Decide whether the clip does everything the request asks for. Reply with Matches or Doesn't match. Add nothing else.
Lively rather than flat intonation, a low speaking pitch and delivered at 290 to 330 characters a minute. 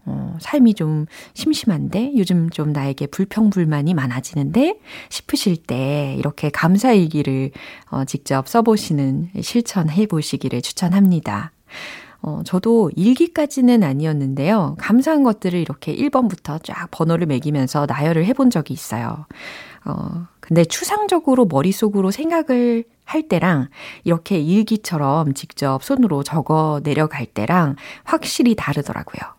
Doesn't match